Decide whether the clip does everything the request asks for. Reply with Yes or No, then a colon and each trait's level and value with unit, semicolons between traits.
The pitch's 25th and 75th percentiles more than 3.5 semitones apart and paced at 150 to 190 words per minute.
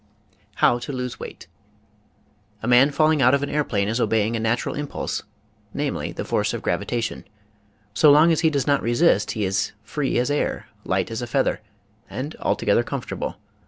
Yes: average, 4.2 semitones; average, 180 wpm